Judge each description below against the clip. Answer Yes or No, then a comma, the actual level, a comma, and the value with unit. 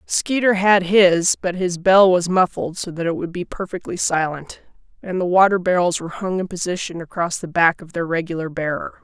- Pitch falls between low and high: Yes, medium, 180 Hz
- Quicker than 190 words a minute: Yes, average, 200 wpm